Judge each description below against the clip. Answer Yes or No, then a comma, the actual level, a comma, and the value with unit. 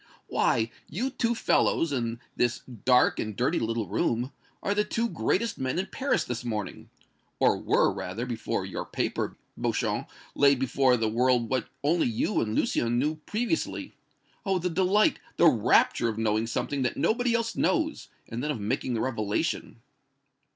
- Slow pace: No, average, 165 wpm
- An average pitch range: No, wide, 8.0 semitones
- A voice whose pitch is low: Yes, low, 130 Hz